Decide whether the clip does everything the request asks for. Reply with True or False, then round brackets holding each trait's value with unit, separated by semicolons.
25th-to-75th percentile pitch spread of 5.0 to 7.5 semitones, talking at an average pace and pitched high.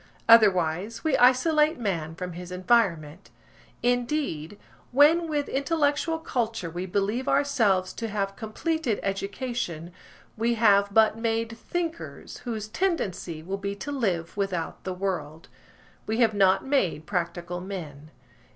False (5.5 semitones; 125 wpm; 205 Hz)